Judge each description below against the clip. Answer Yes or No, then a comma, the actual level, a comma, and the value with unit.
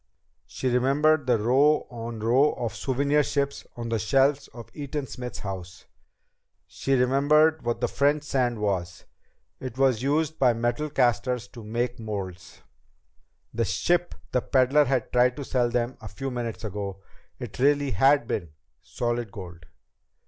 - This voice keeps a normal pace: Yes, average, 150 wpm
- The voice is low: Yes, low, 125 Hz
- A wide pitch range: No, average, 3.4 semitones